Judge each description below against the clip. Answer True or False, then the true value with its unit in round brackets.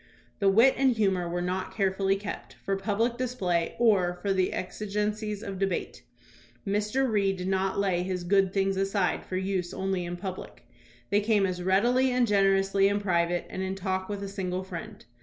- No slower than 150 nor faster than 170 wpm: False (180 wpm)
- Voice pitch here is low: False (195 Hz)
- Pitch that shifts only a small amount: True (1.8 semitones)